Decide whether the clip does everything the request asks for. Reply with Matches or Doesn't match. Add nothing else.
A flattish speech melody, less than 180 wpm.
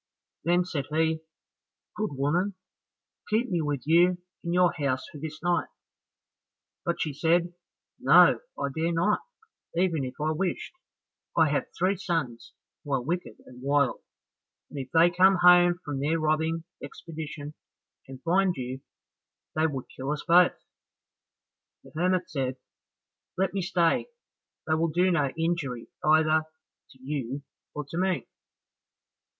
Doesn't match